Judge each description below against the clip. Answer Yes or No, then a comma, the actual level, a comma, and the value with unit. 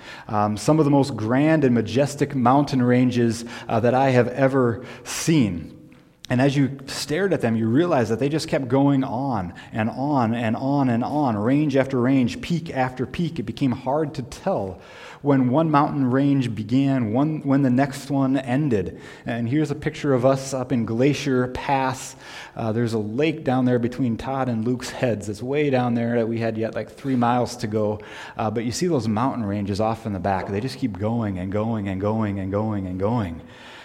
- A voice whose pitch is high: No, low, 125 Hz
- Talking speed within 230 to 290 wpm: No, fast, 205 wpm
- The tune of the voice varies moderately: Yes, average, 3.3 semitones